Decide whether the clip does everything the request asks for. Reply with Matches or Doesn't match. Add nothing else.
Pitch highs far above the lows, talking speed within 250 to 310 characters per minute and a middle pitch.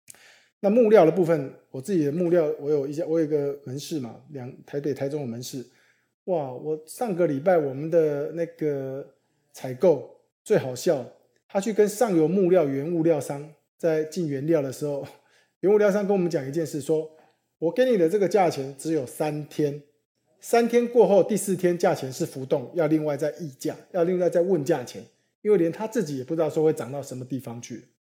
Doesn't match